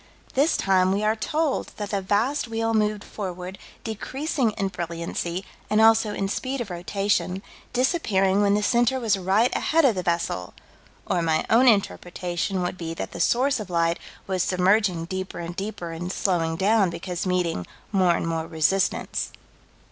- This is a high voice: Yes, high, 195 Hz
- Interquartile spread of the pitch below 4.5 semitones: Yes, average, 3.9 semitones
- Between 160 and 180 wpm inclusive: Yes, average, 165 wpm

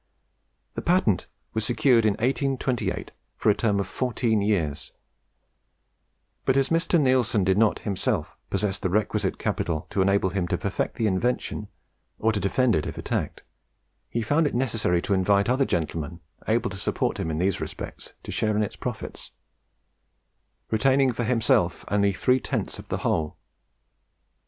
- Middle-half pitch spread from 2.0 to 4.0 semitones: No, average, 4.8 semitones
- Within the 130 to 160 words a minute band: Yes, average, 155 wpm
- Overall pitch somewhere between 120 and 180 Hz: No, low, 110 Hz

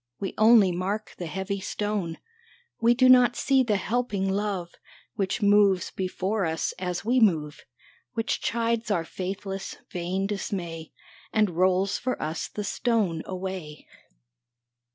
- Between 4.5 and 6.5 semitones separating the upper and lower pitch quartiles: No, average, 3.1 semitones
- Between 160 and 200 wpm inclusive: No, slow, 135 wpm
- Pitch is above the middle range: Yes, high, 195 Hz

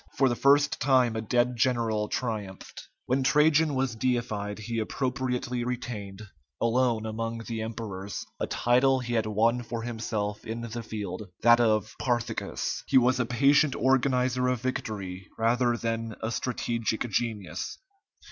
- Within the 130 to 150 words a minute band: Yes, average, 145 wpm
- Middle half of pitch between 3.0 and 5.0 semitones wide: No, narrow, 2.4 semitones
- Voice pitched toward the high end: No, low, 120 Hz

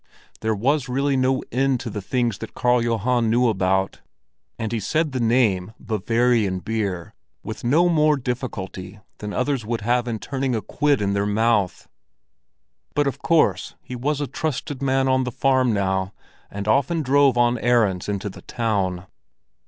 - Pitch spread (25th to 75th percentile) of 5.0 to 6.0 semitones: No, average, 4.2 semitones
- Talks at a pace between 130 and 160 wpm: No, average, 170 wpm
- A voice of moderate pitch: No, low, 120 Hz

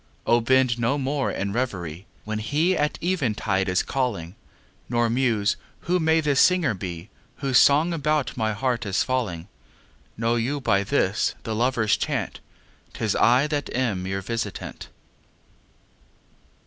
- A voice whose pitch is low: Yes, low, 120 Hz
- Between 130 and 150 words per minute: Yes, average, 140 wpm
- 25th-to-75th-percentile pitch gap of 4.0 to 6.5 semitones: Yes, wide, 5.5 semitones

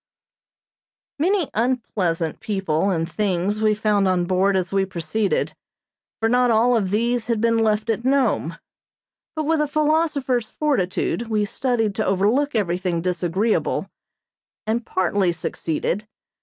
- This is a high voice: Yes, high, 215 Hz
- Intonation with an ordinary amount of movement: Yes, average, 4.5 semitones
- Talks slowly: Yes, slow, 130 wpm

